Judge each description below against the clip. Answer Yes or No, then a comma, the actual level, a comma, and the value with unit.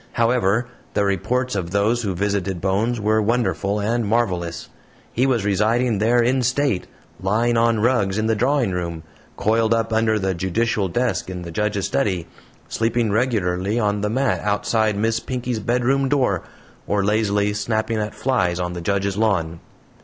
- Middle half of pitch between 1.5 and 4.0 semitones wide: Yes, average, 3.2 semitones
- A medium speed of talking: Yes, average, 160 wpm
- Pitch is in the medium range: No, low, 110 Hz